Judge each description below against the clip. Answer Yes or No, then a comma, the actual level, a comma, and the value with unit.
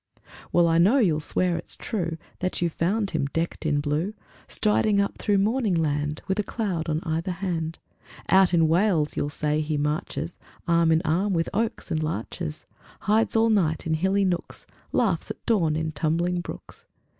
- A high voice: No, medium, 170 Hz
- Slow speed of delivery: No, average, 180 wpm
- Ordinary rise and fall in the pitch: Yes, average, 3.9 semitones